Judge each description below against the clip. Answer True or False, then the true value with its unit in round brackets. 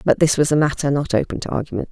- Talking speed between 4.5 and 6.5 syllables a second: False (7.2 syllables/s)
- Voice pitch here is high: False (140 Hz)